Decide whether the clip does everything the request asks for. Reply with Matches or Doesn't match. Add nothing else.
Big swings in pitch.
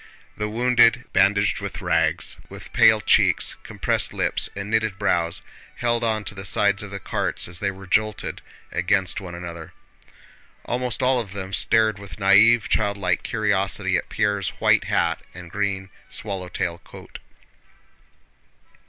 Doesn't match